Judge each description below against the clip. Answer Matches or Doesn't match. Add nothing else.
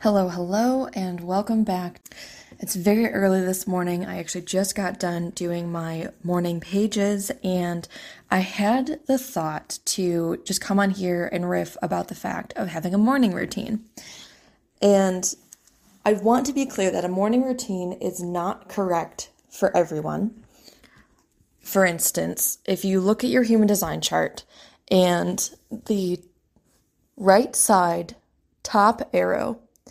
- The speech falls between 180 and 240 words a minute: Doesn't match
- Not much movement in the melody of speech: Doesn't match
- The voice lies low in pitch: Doesn't match